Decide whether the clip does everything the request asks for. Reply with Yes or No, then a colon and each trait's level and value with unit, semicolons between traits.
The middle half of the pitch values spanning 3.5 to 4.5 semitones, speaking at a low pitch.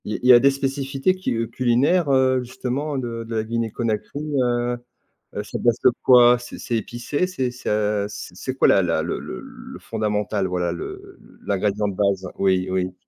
Yes: average, 3.9 semitones; low, 115 Hz